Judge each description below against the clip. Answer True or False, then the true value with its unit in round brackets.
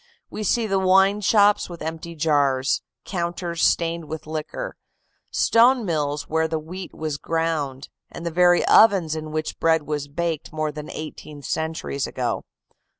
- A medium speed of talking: True (150 wpm)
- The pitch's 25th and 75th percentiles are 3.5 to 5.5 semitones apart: False (2.7 semitones)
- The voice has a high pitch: False (160 Hz)